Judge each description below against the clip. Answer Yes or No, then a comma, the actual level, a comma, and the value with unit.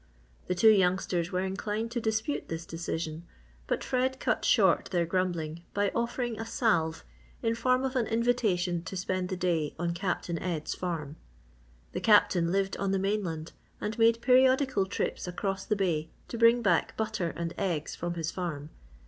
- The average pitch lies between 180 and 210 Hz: Yes, high, 190 Hz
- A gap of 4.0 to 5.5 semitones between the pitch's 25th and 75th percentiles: Yes, average, 4.8 semitones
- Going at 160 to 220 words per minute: Yes, average, 170 wpm